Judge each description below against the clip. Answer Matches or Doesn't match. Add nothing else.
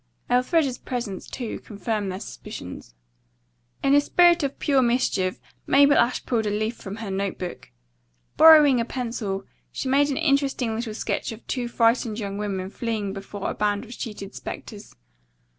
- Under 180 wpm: Matches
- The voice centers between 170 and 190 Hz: Doesn't match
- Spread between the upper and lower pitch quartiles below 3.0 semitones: Doesn't match